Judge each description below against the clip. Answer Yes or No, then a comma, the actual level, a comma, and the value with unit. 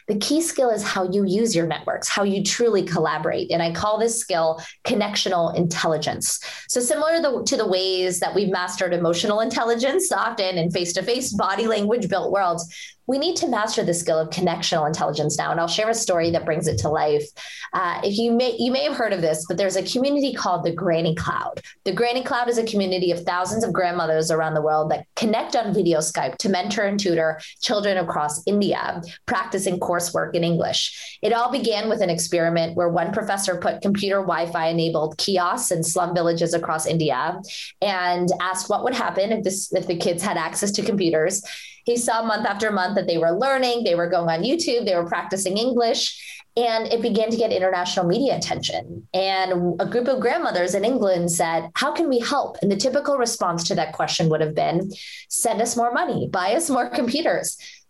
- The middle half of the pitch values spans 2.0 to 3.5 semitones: No, average, 4.9 semitones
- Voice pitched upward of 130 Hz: Yes, high, 190 Hz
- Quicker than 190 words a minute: Yes, fast, 205 wpm